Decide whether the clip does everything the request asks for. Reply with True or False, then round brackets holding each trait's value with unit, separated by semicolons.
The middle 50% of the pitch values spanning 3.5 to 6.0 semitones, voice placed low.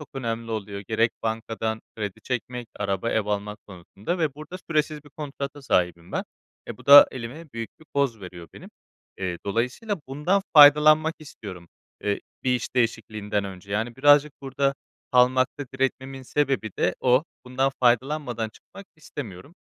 True (5.2 semitones; 125 Hz)